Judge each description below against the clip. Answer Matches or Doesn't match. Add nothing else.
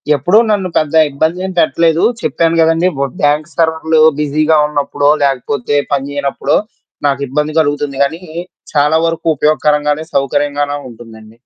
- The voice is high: Doesn't match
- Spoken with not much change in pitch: Matches